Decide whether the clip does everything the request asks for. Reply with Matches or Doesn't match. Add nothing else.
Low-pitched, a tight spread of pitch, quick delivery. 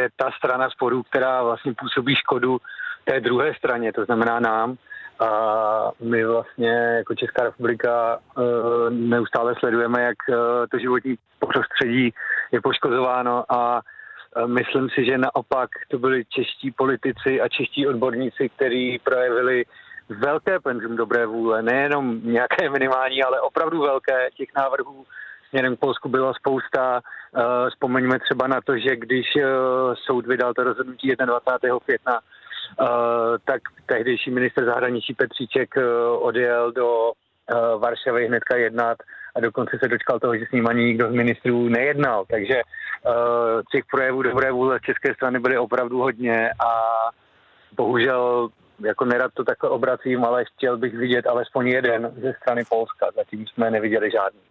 Doesn't match